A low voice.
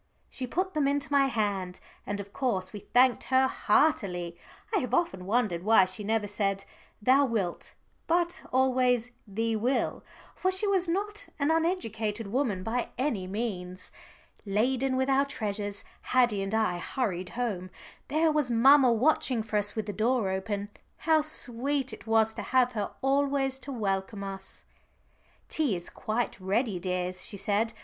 No: high, 230 Hz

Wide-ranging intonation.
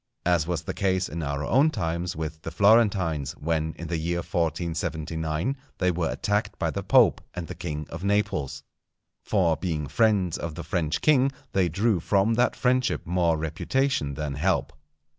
No: average, 3.8 semitones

